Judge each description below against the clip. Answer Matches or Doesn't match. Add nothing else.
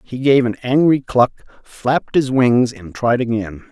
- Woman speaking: Doesn't match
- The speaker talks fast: Doesn't match